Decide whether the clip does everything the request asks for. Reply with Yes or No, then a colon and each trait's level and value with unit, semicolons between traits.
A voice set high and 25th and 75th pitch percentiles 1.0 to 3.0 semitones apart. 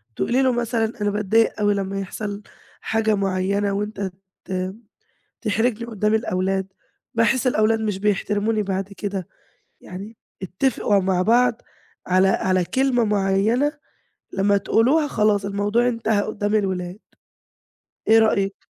Yes: high, 205 Hz; narrow, 2.5 semitones